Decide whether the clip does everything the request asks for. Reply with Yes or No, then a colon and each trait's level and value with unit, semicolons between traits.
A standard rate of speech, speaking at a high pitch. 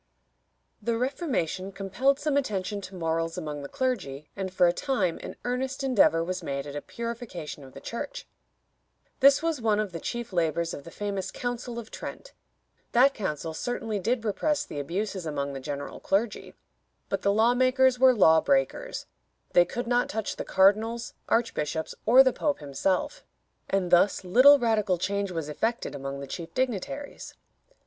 Yes: average, 170 wpm; high, 205 Hz